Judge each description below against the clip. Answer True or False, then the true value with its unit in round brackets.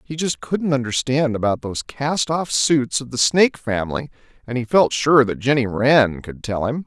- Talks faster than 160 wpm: True (200 wpm)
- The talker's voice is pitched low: True (130 Hz)